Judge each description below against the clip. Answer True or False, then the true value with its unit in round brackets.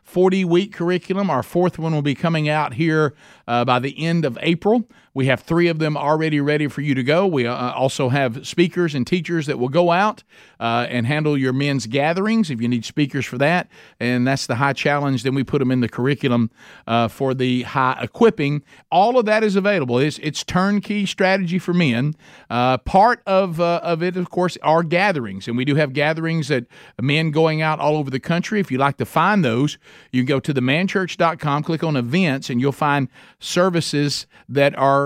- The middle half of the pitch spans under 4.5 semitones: False (4.8 semitones)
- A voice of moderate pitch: True (150 Hz)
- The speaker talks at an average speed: False (210 wpm)